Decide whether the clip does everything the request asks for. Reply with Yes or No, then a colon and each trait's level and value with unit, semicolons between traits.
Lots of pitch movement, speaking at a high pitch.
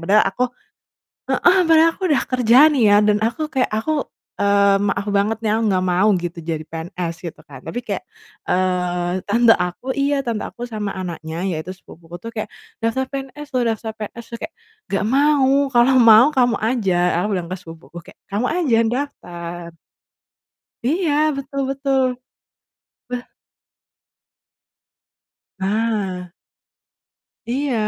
Yes: wide, 6.0 semitones; high, 215 Hz